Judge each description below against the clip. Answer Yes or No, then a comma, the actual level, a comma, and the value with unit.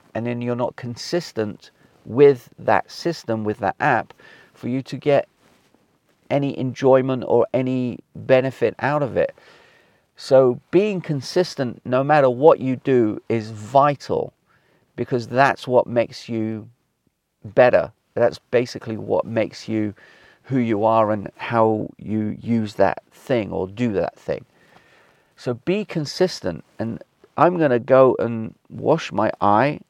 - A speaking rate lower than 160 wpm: Yes, slow, 135 wpm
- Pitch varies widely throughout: No, average, 3.8 semitones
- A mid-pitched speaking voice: No, low, 125 Hz